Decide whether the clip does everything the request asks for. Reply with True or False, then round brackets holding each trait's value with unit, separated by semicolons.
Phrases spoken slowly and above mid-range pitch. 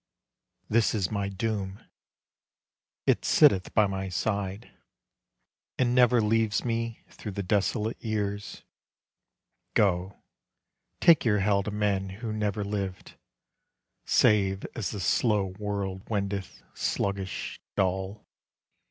False (110 wpm; 100 Hz)